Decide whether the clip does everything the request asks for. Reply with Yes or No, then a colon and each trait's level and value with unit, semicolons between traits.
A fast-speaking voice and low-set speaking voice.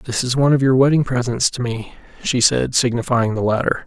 Yes: fast, 215 wpm; low, 125 Hz